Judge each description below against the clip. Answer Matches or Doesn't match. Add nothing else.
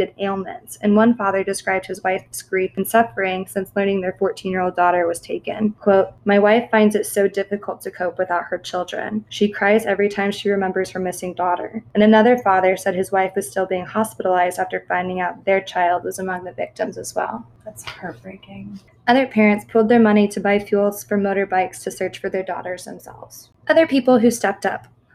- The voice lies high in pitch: Matches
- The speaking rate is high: Doesn't match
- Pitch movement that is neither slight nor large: Doesn't match